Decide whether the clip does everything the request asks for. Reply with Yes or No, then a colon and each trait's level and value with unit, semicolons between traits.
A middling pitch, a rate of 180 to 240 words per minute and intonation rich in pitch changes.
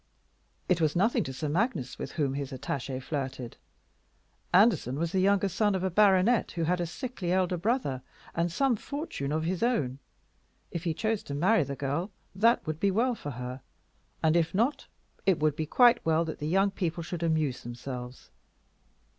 Yes: medium, 170 Hz; average, 185 wpm; wide, 5.7 semitones